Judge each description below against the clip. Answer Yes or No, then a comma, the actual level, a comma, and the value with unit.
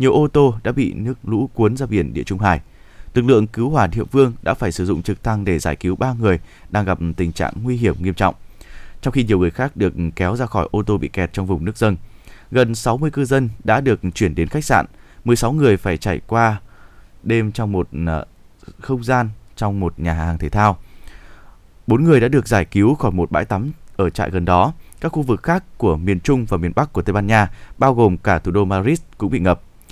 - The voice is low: Yes, low, 105 Hz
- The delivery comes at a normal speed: Yes, average, 235 wpm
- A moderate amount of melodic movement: Yes, average, 5.0 semitones